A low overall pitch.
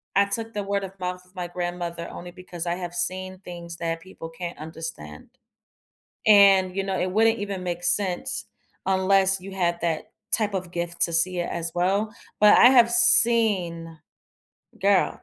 No: medium, 185 Hz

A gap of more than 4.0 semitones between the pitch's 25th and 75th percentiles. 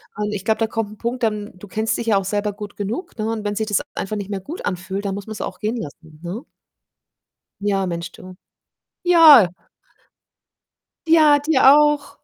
No: average, 3.1 semitones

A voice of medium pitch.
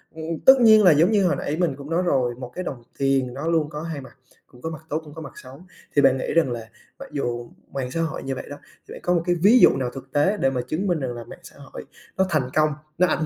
Yes: medium, 150 Hz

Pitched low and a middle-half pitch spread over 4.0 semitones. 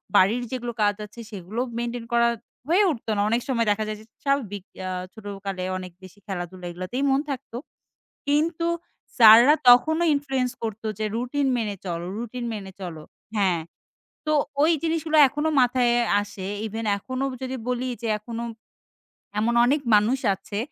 No: high, 235 Hz; average, 4.4 semitones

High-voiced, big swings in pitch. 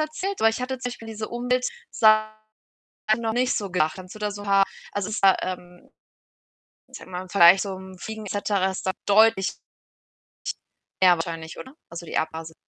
No: high, 205 Hz; average, 3.4 semitones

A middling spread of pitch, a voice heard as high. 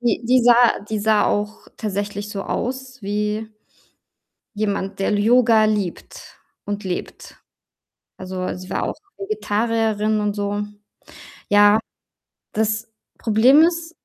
No: narrow, 2.2 semitones; high, 215 Hz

